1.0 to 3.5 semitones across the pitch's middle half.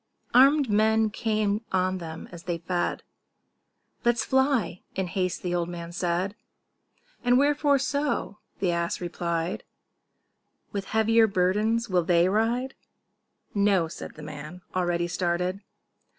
No: average, 4.4 semitones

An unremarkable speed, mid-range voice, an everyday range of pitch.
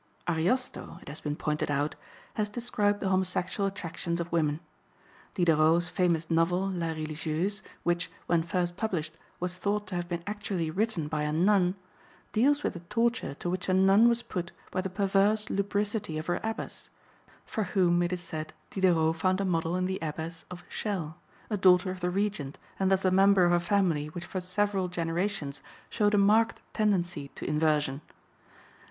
Yes: average, 175 wpm; medium, 180 Hz; average, 3.4 semitones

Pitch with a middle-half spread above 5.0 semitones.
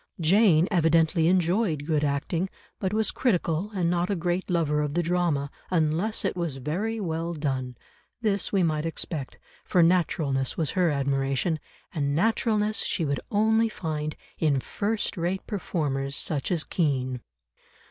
No: average, 4.1 semitones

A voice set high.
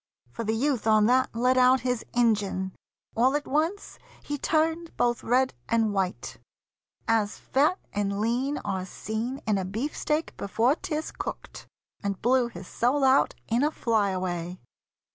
Yes: high, 235 Hz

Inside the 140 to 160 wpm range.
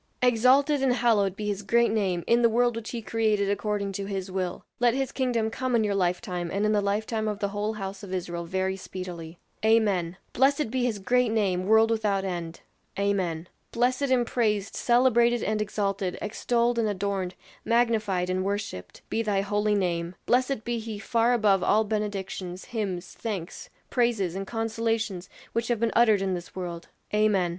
No: average, 180 wpm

